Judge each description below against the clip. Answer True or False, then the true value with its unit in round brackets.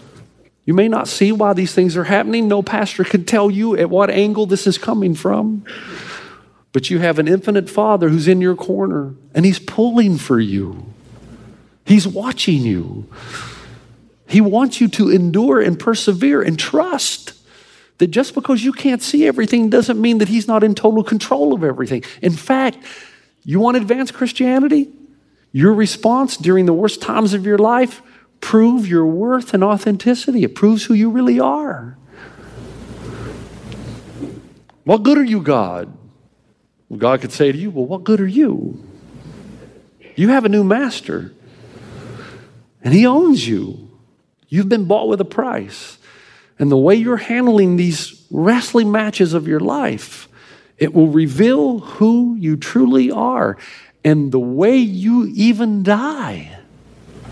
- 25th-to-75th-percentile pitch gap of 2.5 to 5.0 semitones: False (5.6 semitones)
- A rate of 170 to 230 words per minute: False (155 wpm)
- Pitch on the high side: True (205 Hz)